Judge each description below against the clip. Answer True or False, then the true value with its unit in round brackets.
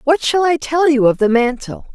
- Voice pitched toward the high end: True (280 Hz)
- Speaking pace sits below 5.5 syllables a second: True (5.0 syllables/s)